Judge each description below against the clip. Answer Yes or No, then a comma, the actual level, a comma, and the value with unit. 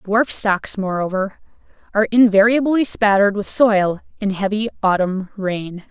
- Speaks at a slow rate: Yes, slow, 120 wpm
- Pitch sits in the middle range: No, high, 205 Hz